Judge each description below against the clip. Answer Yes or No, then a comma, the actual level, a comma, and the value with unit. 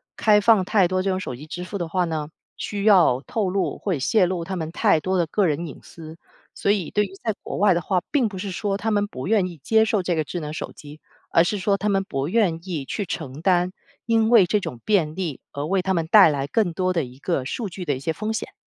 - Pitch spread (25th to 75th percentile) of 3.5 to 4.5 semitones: Yes, average, 4.1 semitones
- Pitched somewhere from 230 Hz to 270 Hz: No, medium, 185 Hz